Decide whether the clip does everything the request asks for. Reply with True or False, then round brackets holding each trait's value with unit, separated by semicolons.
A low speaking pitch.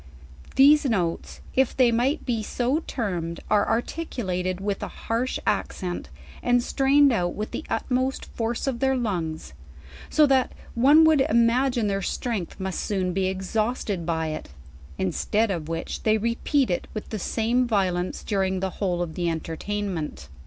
False (215 Hz)